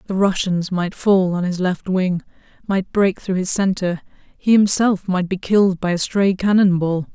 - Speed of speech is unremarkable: Yes, average, 195 wpm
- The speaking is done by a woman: Yes, female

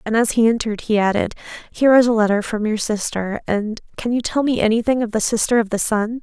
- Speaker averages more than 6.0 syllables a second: Yes, 6.2 syllables/s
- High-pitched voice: Yes, high, 220 Hz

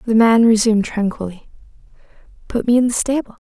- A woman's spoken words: Yes, female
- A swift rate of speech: No, average, 155 wpm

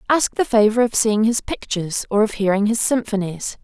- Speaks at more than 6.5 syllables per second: No, 5.3 syllables/s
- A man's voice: No, female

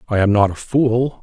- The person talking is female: No, male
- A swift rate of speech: Yes, fast, 245 wpm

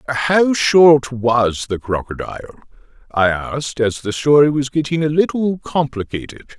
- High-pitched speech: No, low, 135 Hz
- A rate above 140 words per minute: No, slow, 135 wpm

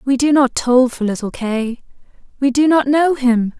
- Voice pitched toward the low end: No, very high, 260 Hz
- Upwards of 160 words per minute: Yes, average, 200 wpm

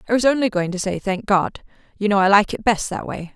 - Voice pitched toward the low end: No, high, 205 Hz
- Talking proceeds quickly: Yes, fast, 285 wpm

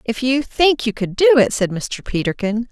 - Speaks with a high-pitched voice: Yes, high, 240 Hz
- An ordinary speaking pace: No, fast, 220 wpm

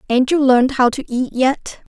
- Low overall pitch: No, very high, 260 Hz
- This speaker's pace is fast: Yes, fast, 215 wpm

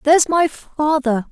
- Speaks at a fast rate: No, slow, 135 wpm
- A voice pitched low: No, very high, 295 Hz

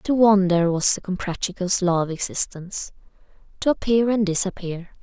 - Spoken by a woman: Yes, female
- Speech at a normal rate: No, slow, 130 wpm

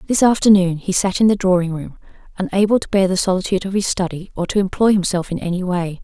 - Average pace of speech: No, fast, 230 wpm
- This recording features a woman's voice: Yes, female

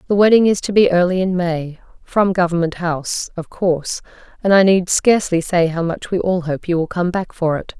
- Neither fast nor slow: No, fast, 225 wpm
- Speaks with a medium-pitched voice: Yes, medium, 180 Hz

